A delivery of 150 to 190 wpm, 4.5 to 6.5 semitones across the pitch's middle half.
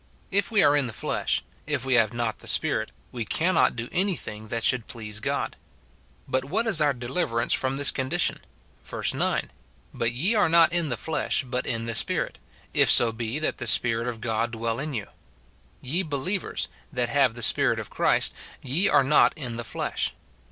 No: average, 200 wpm; average, 4.8 semitones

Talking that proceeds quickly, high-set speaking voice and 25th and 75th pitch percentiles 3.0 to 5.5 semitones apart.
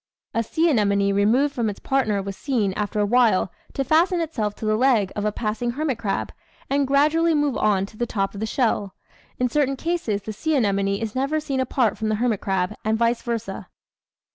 Yes: fast, 210 wpm; high, 230 Hz; average, 4.8 semitones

